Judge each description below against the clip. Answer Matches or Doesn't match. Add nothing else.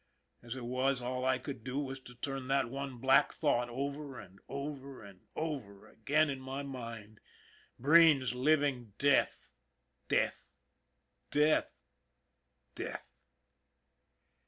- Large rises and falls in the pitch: Doesn't match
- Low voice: Matches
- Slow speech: Matches